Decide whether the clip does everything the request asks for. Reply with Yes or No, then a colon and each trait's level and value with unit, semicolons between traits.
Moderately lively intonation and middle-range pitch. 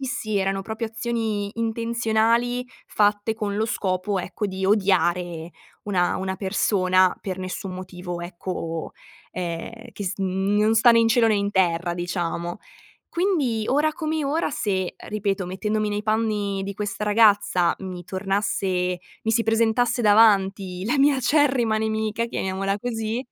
No: average, 3.3 semitones; high, 205 Hz